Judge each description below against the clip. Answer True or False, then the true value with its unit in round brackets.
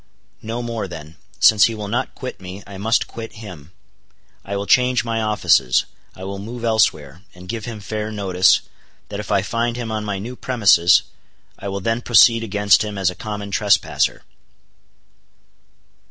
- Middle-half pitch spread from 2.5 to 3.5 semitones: True (3.0 semitones)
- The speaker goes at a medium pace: True (170 wpm)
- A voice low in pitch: True (105 Hz)